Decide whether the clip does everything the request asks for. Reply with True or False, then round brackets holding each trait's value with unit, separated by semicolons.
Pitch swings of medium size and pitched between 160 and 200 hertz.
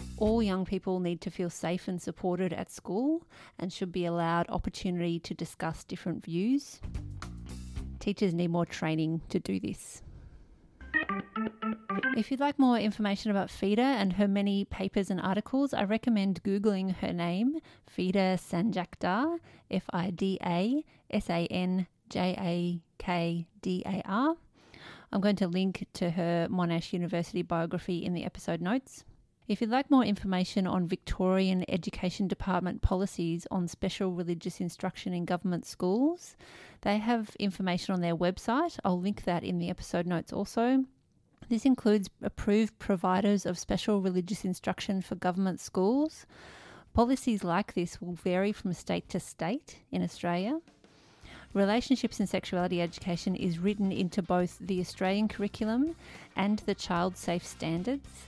True (3.0 semitones; 190 Hz)